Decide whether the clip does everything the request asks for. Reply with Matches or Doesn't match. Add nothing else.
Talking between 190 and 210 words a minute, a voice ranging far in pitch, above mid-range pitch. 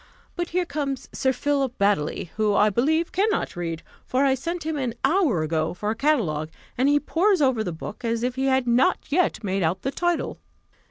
Matches